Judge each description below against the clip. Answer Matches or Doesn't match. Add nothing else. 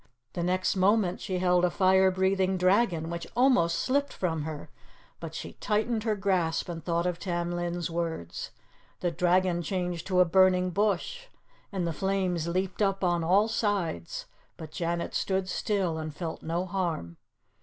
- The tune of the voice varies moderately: Doesn't match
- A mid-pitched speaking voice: Matches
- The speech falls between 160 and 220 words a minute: Matches